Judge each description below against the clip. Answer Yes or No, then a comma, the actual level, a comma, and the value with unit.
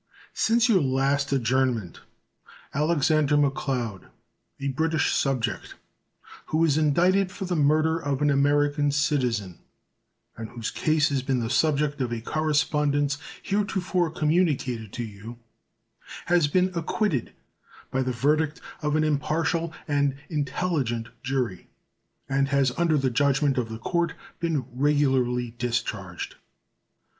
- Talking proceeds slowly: Yes, slow, 125 wpm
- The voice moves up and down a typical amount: Yes, average, 3.5 semitones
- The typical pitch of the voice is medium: Yes, medium, 145 Hz